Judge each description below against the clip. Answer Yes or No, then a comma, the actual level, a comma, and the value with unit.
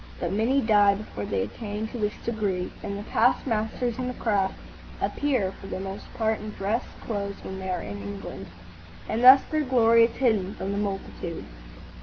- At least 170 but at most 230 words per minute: Yes, average, 190 wpm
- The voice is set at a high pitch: Yes, high, 210 Hz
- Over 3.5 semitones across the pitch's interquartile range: No, average, 3.2 semitones